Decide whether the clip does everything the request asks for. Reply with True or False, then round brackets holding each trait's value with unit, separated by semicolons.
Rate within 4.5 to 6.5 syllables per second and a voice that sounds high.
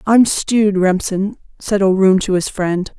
False (4.2 syllables/s; 200 Hz)